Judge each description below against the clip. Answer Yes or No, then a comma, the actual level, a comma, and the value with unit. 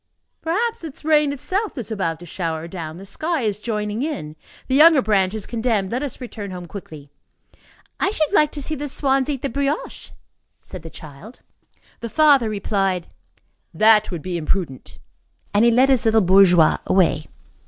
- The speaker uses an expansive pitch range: Yes, wide, 7.3 semitones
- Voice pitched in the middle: No, high, 220 Hz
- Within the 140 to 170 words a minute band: No, average, 180 wpm